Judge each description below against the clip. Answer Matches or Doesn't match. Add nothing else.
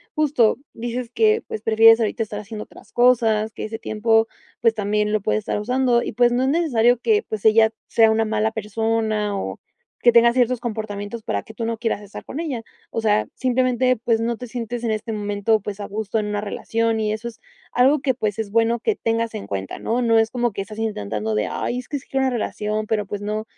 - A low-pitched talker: Doesn't match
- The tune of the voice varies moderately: Doesn't match